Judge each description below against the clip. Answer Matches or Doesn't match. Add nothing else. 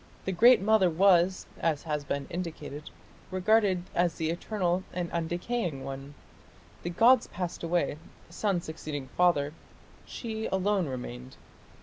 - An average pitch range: Matches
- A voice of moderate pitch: Matches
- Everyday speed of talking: Doesn't match